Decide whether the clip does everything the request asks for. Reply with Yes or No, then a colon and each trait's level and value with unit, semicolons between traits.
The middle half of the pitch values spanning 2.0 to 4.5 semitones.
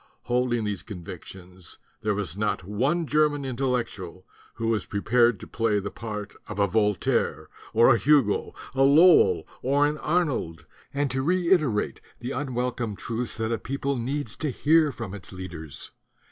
No: average, 5.3 semitones